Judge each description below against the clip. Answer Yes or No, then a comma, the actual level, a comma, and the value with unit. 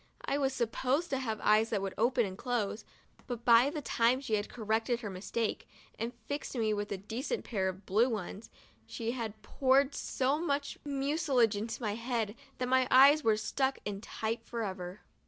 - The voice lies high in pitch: Yes, high, 235 Hz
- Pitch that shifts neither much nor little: Yes, average, 3.7 semitones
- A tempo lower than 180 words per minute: No, average, 190 wpm